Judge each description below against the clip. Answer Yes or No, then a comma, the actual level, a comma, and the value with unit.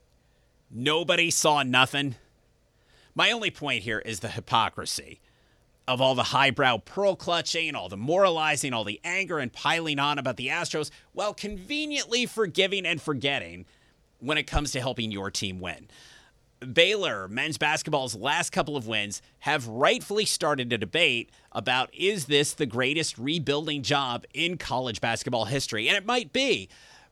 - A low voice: No, medium, 145 Hz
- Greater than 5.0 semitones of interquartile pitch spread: Yes, wide, 5.4 semitones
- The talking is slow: No, average, 150 wpm